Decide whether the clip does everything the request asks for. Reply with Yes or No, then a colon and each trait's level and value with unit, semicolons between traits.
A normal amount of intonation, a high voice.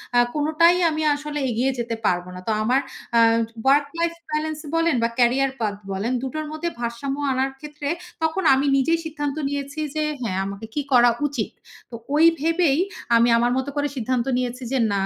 Yes: average, 4.1 semitones; very high, 275 Hz